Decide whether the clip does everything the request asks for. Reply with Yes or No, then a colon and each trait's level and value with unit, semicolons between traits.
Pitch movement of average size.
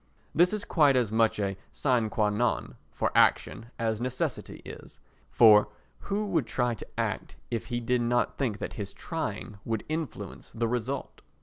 Yes: average, 3.6 semitones